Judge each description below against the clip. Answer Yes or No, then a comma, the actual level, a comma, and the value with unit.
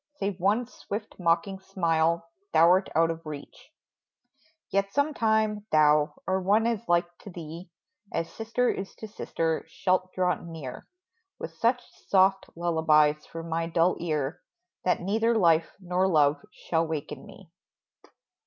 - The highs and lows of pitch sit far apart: No, average, 3.4 semitones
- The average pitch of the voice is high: No, medium, 180 Hz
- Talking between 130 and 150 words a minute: Yes, average, 140 wpm